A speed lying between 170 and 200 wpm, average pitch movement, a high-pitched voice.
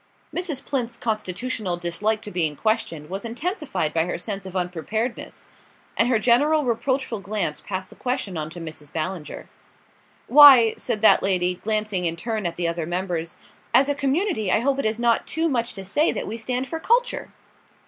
No: average, 180 wpm; wide, 6.2 semitones; high, 215 Hz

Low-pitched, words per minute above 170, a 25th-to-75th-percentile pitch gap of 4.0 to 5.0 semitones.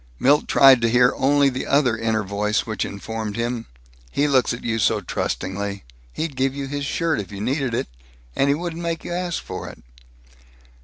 Yes: low, 125 Hz; average, 195 wpm; average, 4.4 semitones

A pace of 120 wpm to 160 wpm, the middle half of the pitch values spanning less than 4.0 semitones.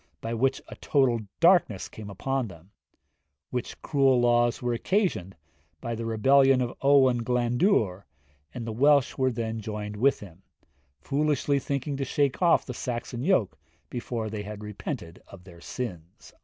No: average, 150 wpm; average, 4.3 semitones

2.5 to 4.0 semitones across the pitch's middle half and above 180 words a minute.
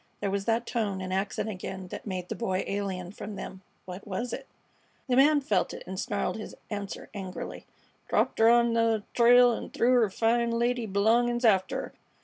Yes: average, 3.7 semitones; average, 190 wpm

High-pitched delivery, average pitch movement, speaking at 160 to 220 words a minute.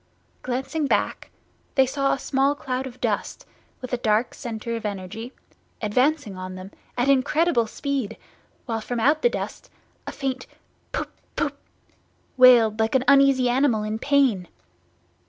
No: very high, 255 Hz; average, 3.7 semitones; average, 145 wpm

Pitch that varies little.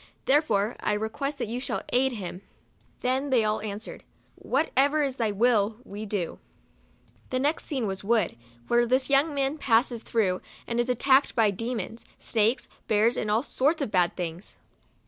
No: average, 4.1 semitones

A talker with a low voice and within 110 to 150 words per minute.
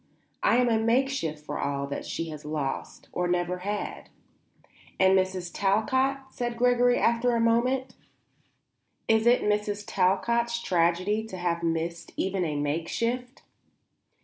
No: high, 205 Hz; slow, 135 wpm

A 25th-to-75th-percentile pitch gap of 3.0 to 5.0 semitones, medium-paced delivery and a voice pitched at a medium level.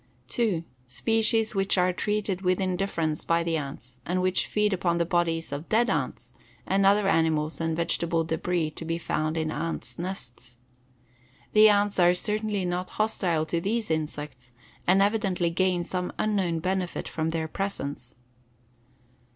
Yes: average, 3.4 semitones; average, 150 wpm; medium, 175 Hz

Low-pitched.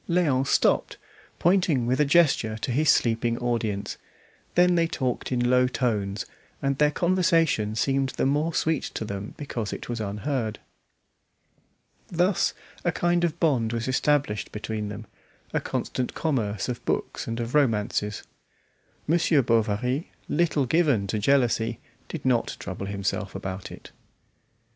Yes: low, 125 Hz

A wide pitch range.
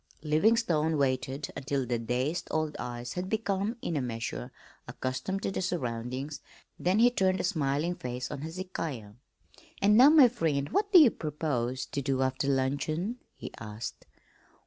Yes: wide, 6.4 semitones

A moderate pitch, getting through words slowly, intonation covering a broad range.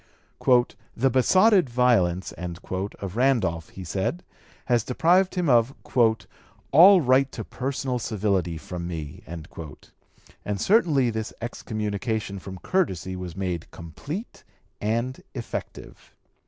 No: low, 110 Hz; slow, 105 wpm; wide, 6.4 semitones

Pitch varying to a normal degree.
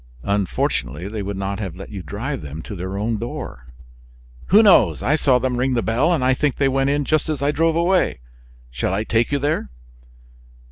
No: wide, 6.7 semitones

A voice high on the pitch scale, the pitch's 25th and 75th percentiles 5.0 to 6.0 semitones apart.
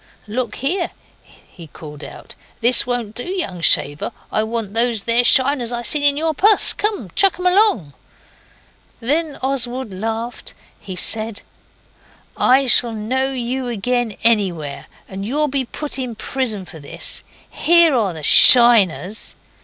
No: high, 240 Hz; average, 4.5 semitones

